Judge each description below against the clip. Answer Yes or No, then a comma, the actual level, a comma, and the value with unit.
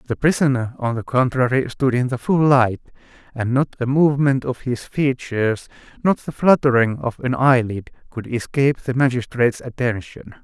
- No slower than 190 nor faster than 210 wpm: No, average, 160 wpm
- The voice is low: Yes, low, 125 Hz